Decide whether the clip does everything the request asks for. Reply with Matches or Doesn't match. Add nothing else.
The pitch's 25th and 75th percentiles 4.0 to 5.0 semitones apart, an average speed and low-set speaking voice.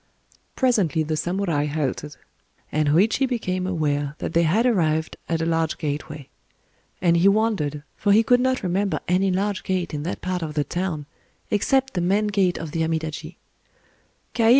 Doesn't match